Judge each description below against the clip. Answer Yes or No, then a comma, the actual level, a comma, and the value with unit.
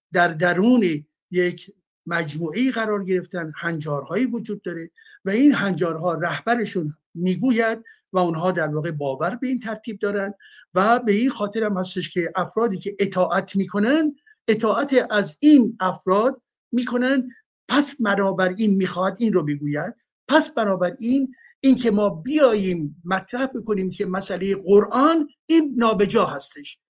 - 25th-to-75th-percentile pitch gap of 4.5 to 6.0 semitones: Yes, average, 5.2 semitones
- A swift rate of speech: No, average, 135 wpm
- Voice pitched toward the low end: No, high, 200 Hz